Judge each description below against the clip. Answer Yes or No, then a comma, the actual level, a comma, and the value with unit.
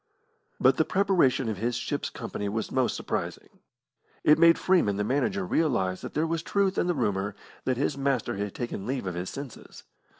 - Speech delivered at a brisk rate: No, average, 190 wpm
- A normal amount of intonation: No, wide, 8.0 semitones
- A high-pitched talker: No, low, 130 Hz